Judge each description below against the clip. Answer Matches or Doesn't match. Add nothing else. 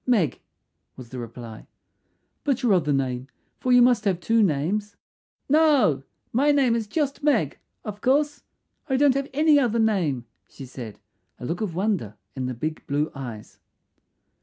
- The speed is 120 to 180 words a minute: Matches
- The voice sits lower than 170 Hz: Doesn't match